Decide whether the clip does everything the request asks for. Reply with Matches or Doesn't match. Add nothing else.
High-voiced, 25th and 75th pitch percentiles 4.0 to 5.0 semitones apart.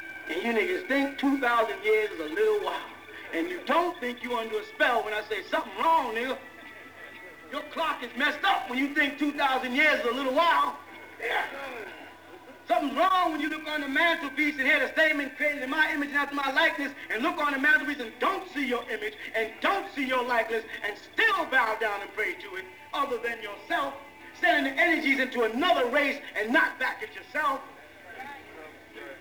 Matches